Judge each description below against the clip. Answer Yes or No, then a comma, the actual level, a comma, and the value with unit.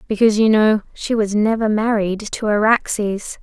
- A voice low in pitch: No, high, 215 Hz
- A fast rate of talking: No, average, 160 wpm